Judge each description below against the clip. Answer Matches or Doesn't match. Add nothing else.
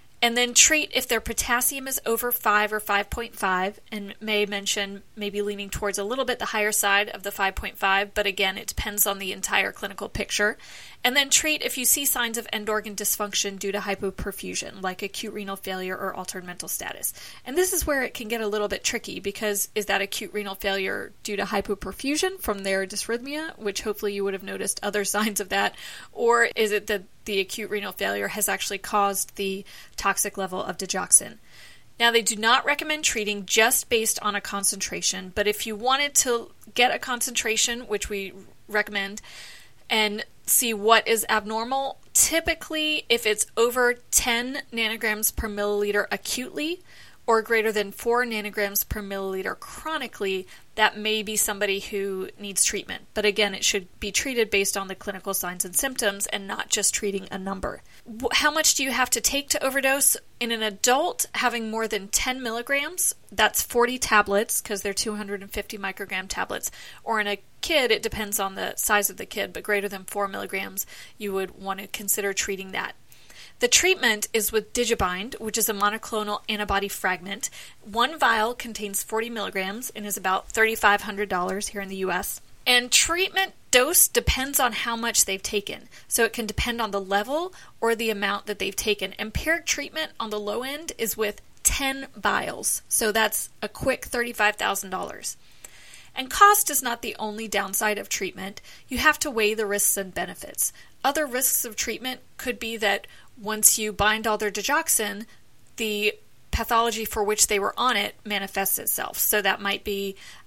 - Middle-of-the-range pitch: Doesn't match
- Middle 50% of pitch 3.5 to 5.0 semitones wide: Doesn't match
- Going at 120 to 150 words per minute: Doesn't match